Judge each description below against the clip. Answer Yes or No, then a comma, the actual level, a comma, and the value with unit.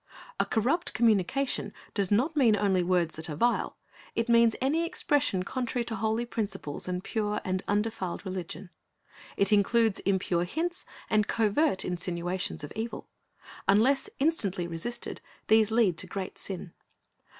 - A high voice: Yes, high, 210 Hz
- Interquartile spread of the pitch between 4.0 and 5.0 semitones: Yes, average, 4.3 semitones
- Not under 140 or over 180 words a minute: Yes, average, 145 wpm